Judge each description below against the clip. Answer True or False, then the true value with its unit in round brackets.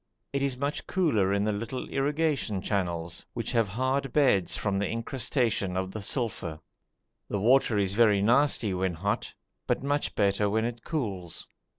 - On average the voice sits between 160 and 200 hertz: False (110 Hz)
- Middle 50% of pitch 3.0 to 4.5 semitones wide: False (5.1 semitones)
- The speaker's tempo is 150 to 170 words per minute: True (165 wpm)